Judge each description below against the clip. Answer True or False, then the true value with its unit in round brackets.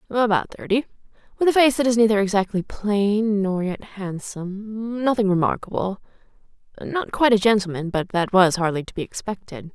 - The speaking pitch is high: True (205 Hz)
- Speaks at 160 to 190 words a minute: False (150 wpm)